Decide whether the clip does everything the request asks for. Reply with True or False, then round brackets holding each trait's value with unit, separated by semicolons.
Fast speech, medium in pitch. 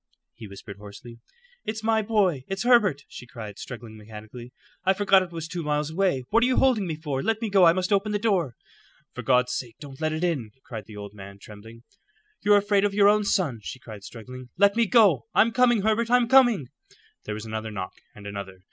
True (215 wpm; 155 Hz)